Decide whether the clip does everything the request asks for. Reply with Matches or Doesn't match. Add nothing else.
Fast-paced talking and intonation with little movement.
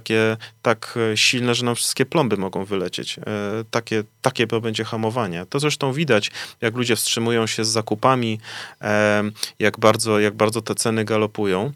Doesn't match